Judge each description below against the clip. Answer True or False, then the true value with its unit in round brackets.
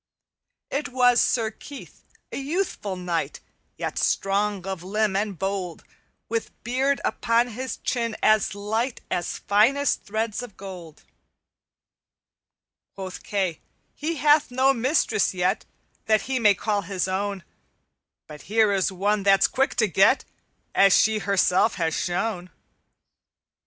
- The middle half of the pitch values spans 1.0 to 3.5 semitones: False (4.1 semitones)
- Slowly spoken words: True (130 wpm)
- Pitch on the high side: True (210 Hz)